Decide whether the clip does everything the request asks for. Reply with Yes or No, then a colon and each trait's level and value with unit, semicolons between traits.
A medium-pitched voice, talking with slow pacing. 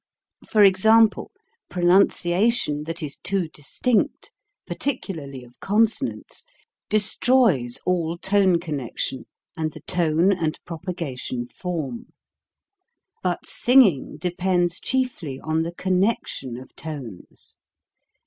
Yes: medium, 175 Hz; slow, 110 wpm